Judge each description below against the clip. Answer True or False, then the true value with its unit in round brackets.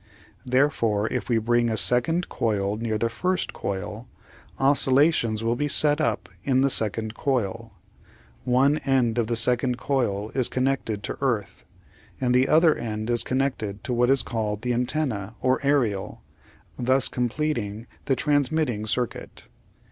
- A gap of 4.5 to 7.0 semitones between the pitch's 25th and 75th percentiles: False (3.7 semitones)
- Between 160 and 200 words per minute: False (150 wpm)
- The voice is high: False (125 Hz)